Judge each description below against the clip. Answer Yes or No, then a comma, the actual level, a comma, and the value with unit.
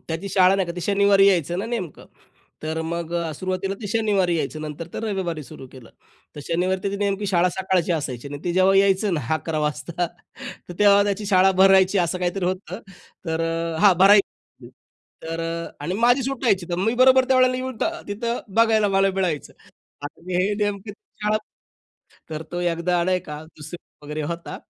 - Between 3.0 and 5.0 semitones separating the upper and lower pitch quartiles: Yes, average, 3.3 semitones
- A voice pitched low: No, medium, 185 Hz